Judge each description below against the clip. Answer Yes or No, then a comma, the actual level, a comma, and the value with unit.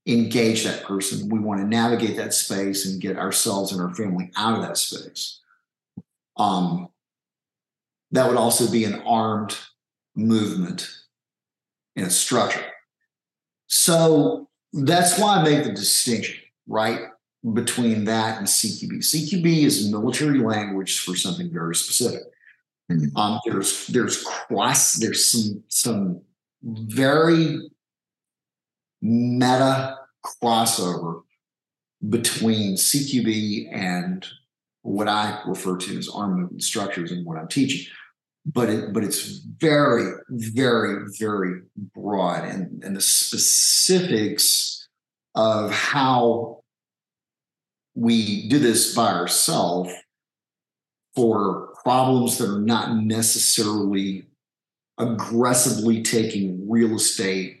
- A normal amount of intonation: Yes, average, 4.5 semitones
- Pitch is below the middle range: Yes, low, 110 Hz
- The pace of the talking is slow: Yes, slow, 110 wpm